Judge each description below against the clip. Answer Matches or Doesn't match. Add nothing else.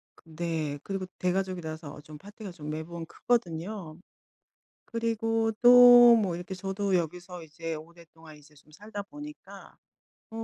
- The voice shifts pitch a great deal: Doesn't match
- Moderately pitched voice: Matches